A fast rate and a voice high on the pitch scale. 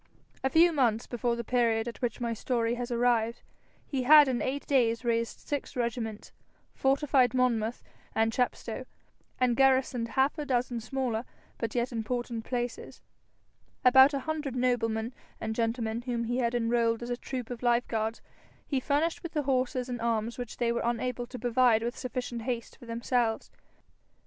No: average, 170 wpm; high, 245 Hz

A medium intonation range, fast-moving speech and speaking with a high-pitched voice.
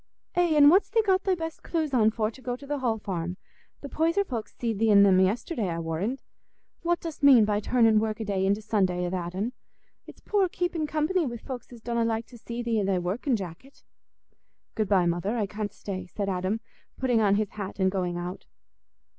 No: wide, 5.9 semitones; fast, 210 wpm; high, 220 Hz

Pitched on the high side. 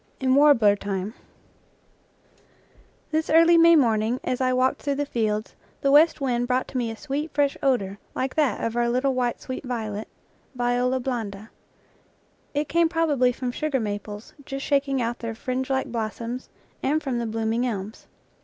Yes: very high, 250 Hz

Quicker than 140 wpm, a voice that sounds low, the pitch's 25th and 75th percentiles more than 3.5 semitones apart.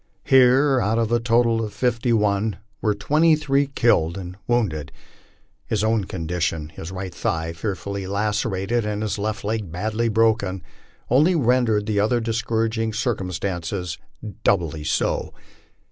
No: slow, 135 wpm; low, 110 Hz; average, 3.9 semitones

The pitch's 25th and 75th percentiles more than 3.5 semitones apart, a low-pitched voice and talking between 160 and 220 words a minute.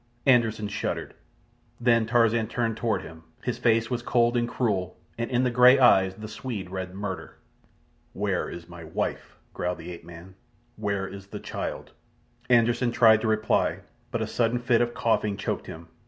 Yes: average, 3.9 semitones; low, 110 Hz; average, 170 wpm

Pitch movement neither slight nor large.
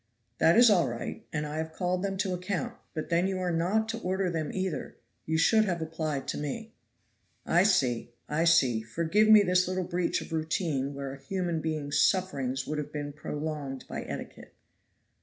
Yes: average, 3.9 semitones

